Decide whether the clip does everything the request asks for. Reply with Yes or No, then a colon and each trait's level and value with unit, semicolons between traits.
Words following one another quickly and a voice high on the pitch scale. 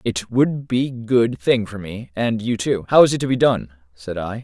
No: fast, 245 wpm; low, 115 Hz